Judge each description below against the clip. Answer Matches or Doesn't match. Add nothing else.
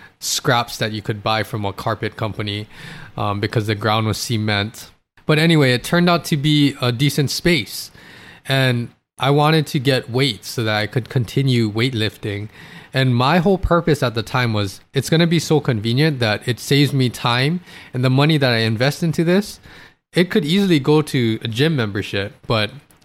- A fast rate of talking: Doesn't match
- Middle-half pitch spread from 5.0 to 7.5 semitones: Matches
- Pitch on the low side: Matches